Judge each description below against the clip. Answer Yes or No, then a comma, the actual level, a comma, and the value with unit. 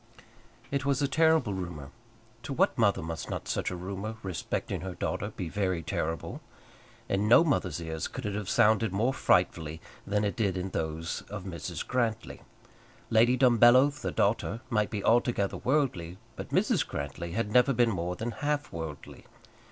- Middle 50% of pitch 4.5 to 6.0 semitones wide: Yes, wide, 5.5 semitones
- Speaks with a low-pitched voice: Yes, low, 100 Hz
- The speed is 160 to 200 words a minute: Yes, average, 165 wpm